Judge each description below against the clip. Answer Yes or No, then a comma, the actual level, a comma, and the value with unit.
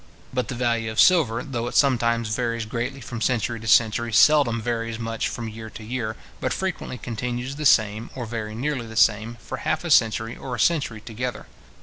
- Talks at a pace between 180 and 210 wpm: Yes, average, 200 wpm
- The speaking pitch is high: No, low, 115 Hz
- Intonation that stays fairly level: Yes, narrow, 2.0 semitones